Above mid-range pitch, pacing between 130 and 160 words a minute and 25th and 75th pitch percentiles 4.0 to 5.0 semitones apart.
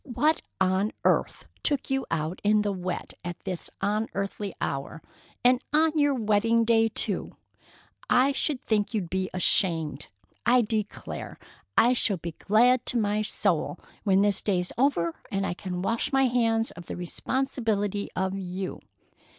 Yes: high, 210 Hz; average, 150 wpm; average, 4.4 semitones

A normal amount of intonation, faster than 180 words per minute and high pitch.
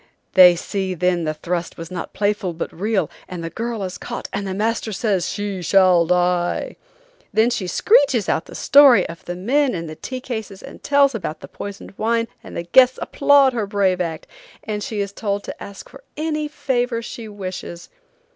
Yes: average, 4.6 semitones; average, 195 wpm; high, 200 Hz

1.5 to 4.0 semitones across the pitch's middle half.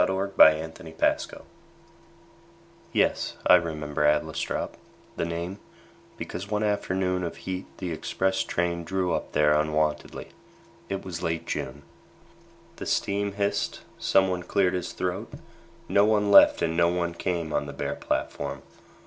Yes: average, 3.0 semitones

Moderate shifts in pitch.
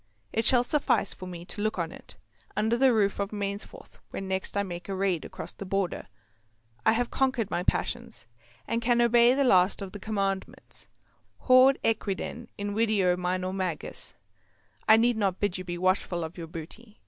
Yes: average, 3.8 semitones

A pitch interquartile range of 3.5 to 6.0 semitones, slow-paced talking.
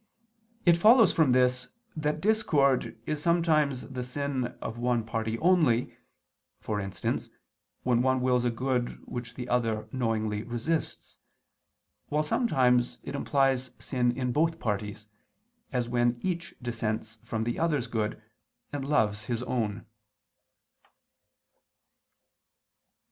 Yes: average, 4.0 semitones; slow, 120 wpm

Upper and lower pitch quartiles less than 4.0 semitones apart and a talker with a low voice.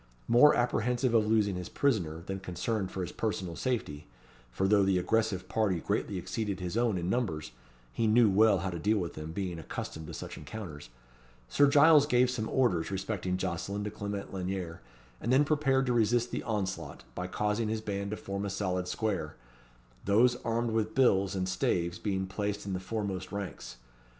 Yes: average, 3.6 semitones; low, 100 Hz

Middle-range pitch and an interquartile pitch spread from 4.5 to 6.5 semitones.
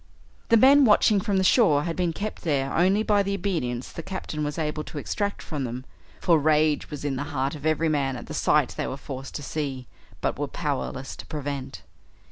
Yes: medium, 150 Hz; average, 5.3 semitones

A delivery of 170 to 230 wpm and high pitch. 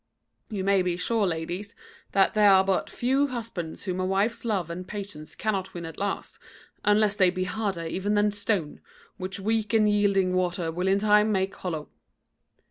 Yes: average, 180 wpm; high, 195 Hz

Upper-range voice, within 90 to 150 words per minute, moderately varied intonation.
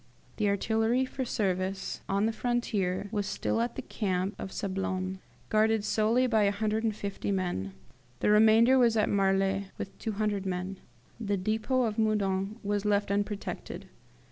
No: high, 205 Hz; average, 145 wpm; narrow, 2.3 semitones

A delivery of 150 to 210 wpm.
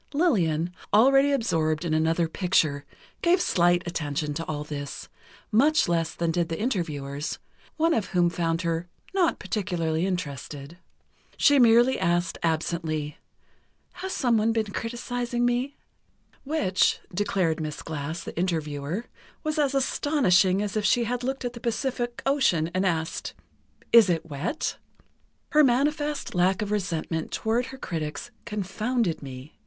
No: average, 140 wpm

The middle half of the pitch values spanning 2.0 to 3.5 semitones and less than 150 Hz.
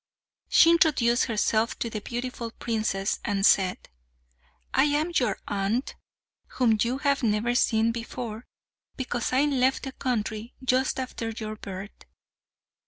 No: average, 3.1 semitones; high, 235 Hz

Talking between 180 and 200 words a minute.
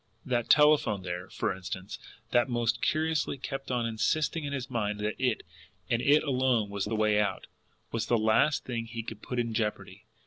Yes: average, 185 wpm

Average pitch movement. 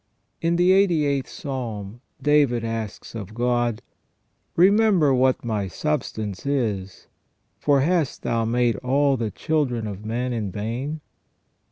Yes: average, 4.7 semitones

